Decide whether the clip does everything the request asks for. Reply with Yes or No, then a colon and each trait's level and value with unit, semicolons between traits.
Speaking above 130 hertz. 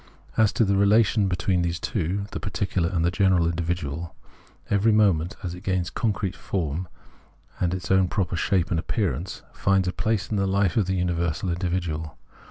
No: very low, 95 Hz